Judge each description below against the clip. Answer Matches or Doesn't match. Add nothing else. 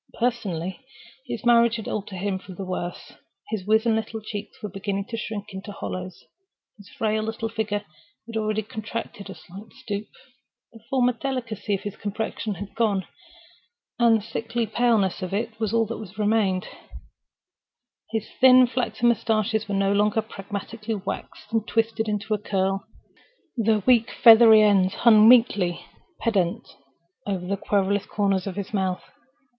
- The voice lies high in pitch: Matches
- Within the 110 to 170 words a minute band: Matches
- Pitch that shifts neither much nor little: Doesn't match